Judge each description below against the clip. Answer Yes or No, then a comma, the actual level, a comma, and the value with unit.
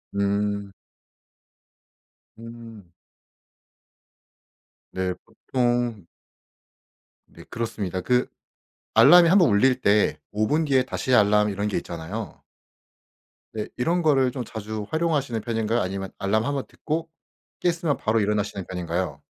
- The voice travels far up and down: No, average, 4.4 semitones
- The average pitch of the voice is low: Yes, low, 110 Hz